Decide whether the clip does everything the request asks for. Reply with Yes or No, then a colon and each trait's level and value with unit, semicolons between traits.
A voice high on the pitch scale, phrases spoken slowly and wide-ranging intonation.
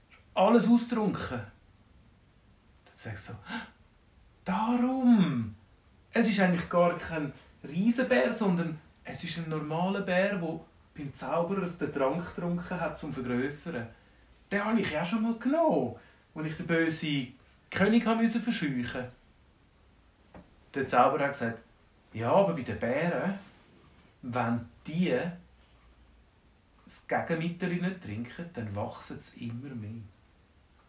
No: medium, 140 Hz; slow, 120 wpm; wide, 8.8 semitones